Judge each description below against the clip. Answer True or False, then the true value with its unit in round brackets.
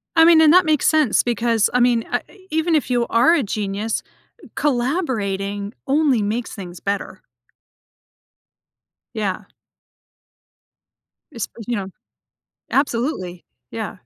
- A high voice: True (235 Hz)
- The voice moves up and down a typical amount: False (6.5 semitones)